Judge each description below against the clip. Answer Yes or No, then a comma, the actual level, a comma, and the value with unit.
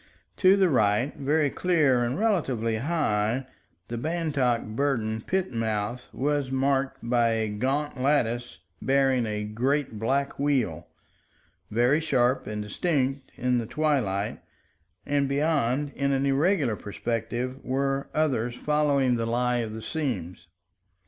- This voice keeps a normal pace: No, slow, 130 wpm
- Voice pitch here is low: Yes, low, 130 Hz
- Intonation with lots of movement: No, average, 3.9 semitones